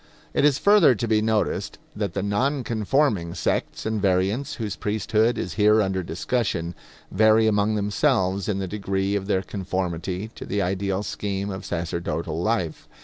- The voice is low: Yes, low, 100 Hz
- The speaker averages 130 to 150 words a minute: No, average, 160 wpm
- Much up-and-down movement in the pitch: No, average, 2.7 semitones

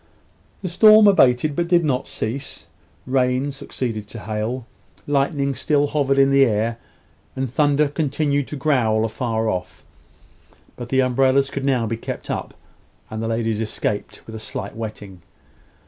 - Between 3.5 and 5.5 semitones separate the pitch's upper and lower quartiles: Yes, average, 4.0 semitones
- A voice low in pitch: Yes, low, 130 Hz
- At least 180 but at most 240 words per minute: No, average, 150 wpm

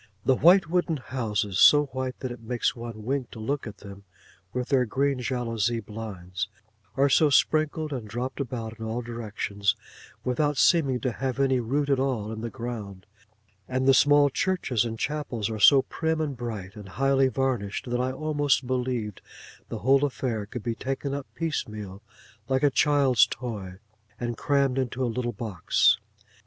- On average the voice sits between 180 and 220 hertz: No, low, 125 Hz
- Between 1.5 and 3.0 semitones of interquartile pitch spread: No, average, 3.7 semitones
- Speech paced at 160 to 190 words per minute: Yes, average, 170 wpm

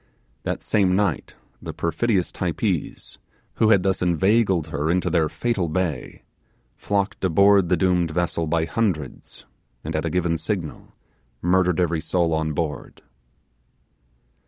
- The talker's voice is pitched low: Yes, very low, 90 Hz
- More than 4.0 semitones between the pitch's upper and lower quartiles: No, average, 2.9 semitones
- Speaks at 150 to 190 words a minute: No, slow, 135 wpm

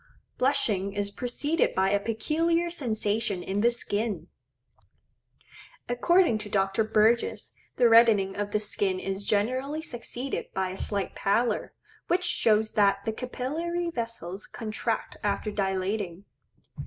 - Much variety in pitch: No, average, 3.7 semitones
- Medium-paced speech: No, slow, 125 wpm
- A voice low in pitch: No, high, 215 Hz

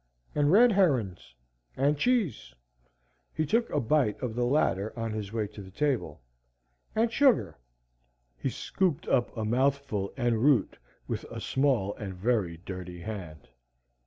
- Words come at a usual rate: Yes, average, 145 wpm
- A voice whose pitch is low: Yes, low, 120 Hz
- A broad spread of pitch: Yes, wide, 6.7 semitones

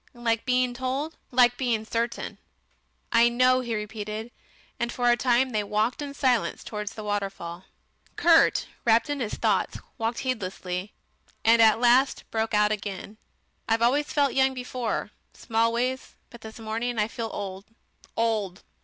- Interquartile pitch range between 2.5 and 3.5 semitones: Yes, average, 2.8 semitones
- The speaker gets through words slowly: No, average, 150 wpm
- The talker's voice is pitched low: No, high, 230 Hz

